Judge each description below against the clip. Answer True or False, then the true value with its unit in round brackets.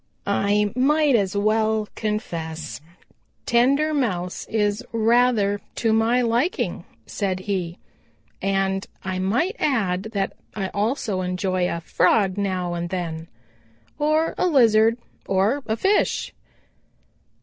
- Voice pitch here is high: True (205 Hz)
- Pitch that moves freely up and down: False (4.0 semitones)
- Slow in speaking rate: True (115 wpm)